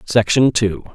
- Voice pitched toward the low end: Yes, low, 110 Hz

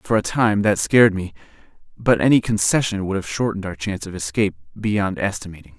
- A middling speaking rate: Yes, average, 185 wpm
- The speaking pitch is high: No, low, 100 Hz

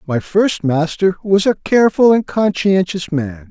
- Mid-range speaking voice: Yes, medium, 180 Hz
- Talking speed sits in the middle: Yes, average, 155 wpm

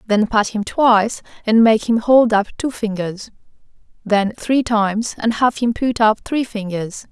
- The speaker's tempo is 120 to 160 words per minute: No, average, 175 wpm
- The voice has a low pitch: No, high, 220 Hz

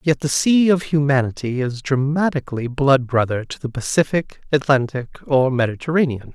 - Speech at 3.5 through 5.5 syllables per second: Yes, 5.2 syllables/s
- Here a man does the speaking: Yes, male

